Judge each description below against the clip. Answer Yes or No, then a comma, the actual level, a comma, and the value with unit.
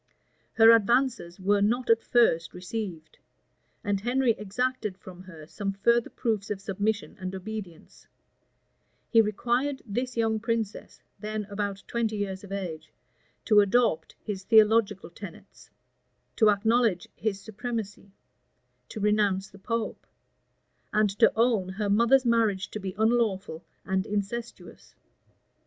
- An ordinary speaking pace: No, slow, 125 wpm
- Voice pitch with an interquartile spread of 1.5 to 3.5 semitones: Yes, average, 2.9 semitones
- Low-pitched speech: No, high, 210 Hz